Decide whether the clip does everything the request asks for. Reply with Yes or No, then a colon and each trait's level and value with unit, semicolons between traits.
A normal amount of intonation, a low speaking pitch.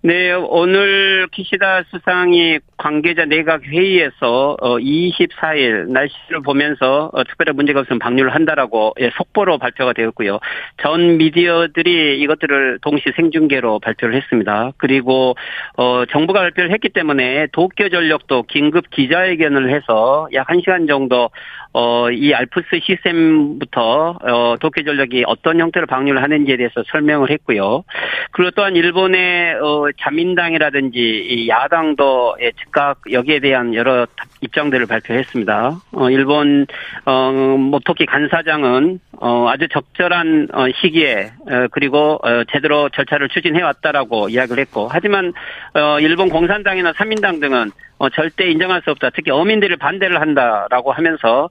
No: average, 4.8 semitones; medium, 150 Hz